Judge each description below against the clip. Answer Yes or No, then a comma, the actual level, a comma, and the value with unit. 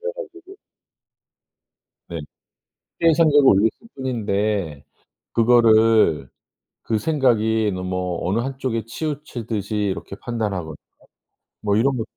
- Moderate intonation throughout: Yes, average, 4.9 semitones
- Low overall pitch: Yes, low, 110 Hz